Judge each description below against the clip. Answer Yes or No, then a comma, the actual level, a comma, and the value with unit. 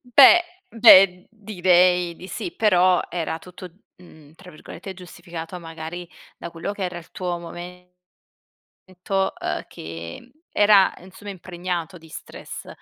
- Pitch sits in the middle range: Yes, medium, 180 Hz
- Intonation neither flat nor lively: No, narrow, 2.3 semitones